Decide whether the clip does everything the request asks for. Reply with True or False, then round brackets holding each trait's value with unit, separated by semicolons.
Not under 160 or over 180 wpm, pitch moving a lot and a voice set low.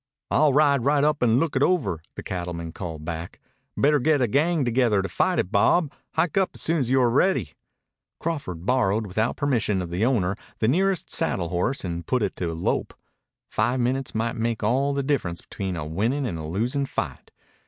False (195 wpm; 7.4 semitones; 120 Hz)